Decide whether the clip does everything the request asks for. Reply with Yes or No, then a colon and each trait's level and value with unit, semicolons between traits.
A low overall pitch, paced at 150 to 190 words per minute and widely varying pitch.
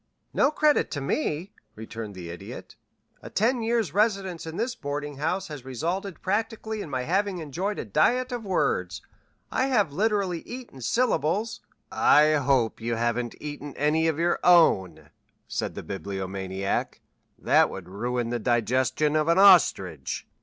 No: medium, 155 Hz; average, 155 wpm; wide, 8.9 semitones